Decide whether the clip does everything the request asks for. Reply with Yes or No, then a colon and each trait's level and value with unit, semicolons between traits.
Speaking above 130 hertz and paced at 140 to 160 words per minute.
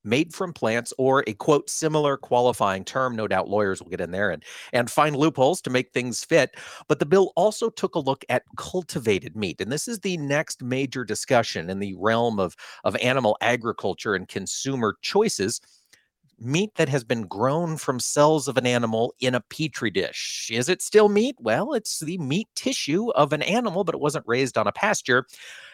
No: medium, 140 Hz; average, 195 wpm